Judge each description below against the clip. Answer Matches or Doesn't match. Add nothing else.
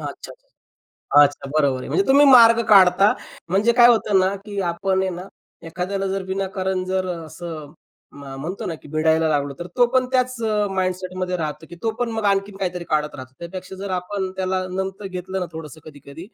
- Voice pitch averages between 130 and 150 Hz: Doesn't match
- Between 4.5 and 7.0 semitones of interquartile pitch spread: Doesn't match